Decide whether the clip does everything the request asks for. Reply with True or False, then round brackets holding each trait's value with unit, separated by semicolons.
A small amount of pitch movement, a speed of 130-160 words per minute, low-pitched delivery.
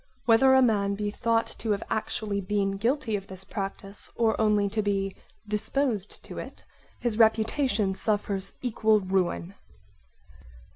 False (2.3 semitones; 140 wpm; 210 Hz)